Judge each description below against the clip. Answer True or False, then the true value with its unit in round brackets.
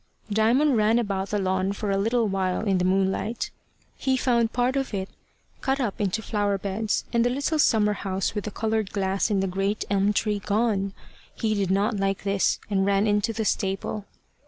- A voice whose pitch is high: True (205 Hz)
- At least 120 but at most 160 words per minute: False (195 wpm)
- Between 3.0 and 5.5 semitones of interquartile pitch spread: False (2.4 semitones)